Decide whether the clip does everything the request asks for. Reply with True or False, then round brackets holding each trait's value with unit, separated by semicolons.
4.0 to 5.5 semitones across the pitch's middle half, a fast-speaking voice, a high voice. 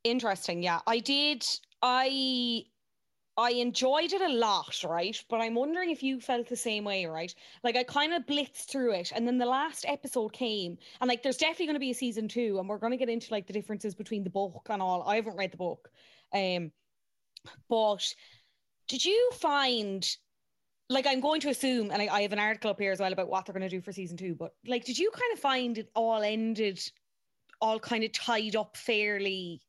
True (4.6 semitones; 220 wpm; 225 Hz)